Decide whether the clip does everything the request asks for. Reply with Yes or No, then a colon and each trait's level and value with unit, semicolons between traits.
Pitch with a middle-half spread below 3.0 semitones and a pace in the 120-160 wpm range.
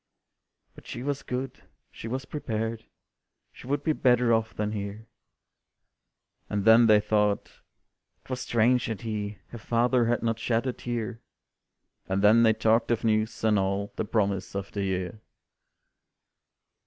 Yes: narrow, 2.4 semitones; average, 150 wpm